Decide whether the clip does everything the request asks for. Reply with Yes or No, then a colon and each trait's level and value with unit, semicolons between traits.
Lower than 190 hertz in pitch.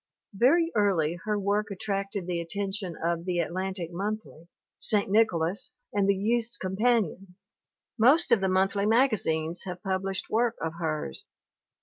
No: high, 195 Hz